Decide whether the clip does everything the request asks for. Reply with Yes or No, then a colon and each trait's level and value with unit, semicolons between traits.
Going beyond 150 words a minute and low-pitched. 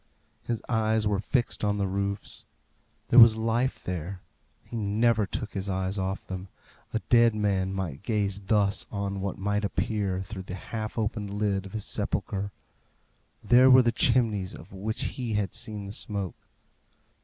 Yes: average, 165 wpm; low, 105 Hz